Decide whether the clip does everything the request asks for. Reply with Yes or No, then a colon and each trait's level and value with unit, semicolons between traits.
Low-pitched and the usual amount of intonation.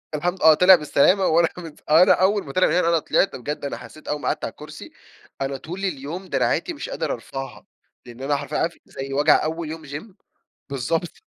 No: medium, 160 Hz; average, 4.1 semitones